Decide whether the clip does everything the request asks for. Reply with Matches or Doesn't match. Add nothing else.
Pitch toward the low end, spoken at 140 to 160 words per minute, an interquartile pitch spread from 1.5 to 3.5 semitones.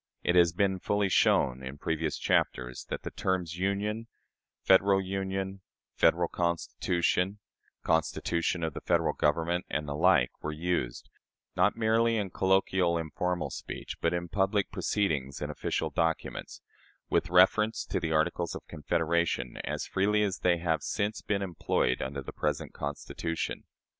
Matches